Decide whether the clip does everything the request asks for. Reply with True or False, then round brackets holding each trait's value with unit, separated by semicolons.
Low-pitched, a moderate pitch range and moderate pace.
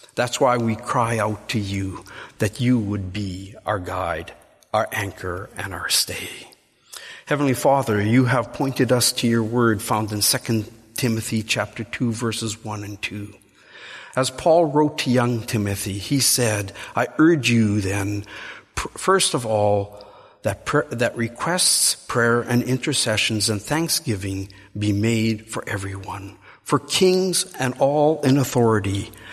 True (110 Hz; 3.7 semitones; 145 wpm)